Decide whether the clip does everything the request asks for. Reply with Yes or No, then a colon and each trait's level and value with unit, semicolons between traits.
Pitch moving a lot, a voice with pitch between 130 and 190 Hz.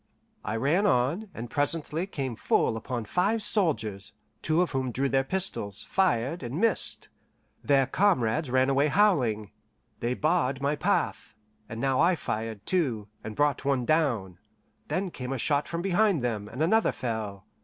Yes: wide, 6.6 semitones; low, 135 Hz